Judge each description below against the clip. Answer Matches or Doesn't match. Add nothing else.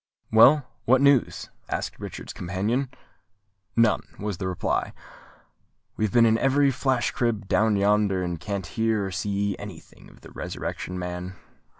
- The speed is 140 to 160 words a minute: Matches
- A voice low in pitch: Matches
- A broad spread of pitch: Doesn't match